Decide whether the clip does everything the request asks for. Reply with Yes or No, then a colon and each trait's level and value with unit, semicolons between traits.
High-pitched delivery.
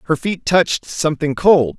No: medium, 160 Hz